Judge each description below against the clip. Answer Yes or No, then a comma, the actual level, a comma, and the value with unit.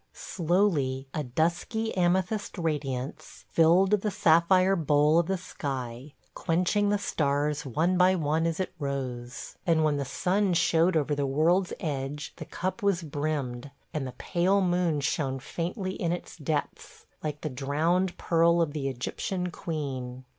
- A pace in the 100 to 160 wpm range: Yes, average, 150 wpm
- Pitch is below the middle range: No, medium, 160 Hz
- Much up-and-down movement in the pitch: No, average, 4.2 semitones